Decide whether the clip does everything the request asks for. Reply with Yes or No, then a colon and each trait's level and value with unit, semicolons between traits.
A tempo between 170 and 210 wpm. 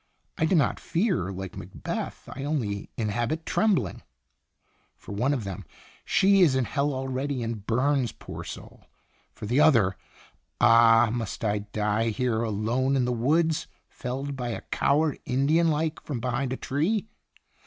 No: average, 160 wpm